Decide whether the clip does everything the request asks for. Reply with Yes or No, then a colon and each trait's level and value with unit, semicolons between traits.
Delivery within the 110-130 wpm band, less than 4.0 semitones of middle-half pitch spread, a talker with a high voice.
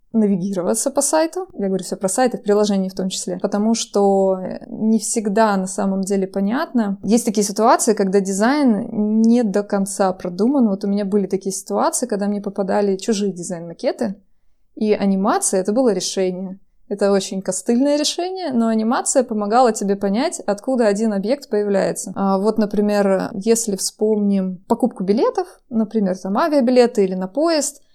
No: average, 155 wpm; average, 3.1 semitones; high, 210 Hz